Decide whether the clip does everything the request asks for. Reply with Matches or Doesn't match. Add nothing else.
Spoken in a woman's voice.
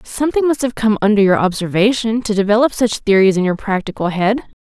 Matches